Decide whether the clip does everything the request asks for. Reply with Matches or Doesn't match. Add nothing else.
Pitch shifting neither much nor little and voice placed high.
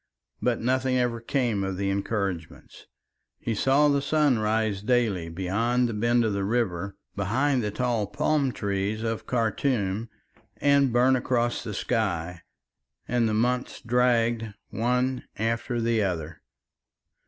Doesn't match